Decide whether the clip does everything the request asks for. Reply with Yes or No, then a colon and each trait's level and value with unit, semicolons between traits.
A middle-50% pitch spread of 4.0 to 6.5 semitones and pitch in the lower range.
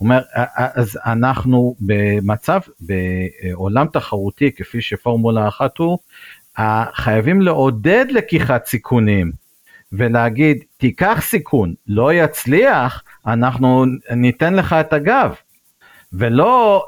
Yes: average, 5.2 semitones; low, 125 Hz